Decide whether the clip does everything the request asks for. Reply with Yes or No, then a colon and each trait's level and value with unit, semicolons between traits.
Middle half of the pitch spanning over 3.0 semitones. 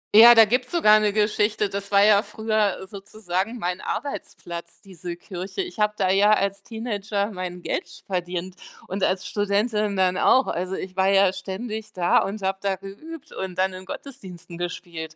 No: narrow, 2.5 semitones